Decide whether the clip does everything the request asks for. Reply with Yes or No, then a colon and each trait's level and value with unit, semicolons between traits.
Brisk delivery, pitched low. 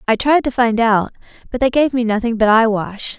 No: fast, 225 wpm; high, 235 Hz